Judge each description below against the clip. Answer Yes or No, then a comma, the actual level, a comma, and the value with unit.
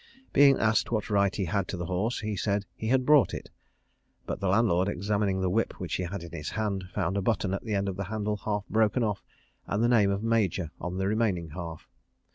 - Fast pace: Yes, fast, 235 wpm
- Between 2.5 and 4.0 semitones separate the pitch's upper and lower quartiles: Yes, average, 2.8 semitones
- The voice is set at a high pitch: No, low, 100 Hz